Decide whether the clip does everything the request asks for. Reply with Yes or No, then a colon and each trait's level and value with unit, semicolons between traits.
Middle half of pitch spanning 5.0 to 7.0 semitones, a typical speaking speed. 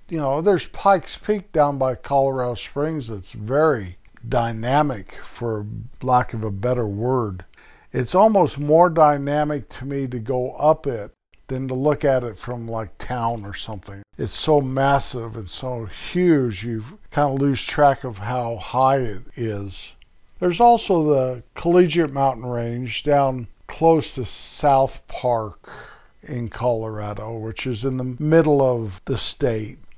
No: average, 4.3 semitones; average, 150 wpm